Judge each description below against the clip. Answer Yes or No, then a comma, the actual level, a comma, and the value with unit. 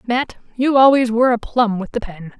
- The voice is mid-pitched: No, high, 235 Hz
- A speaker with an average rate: No, fast, 225 wpm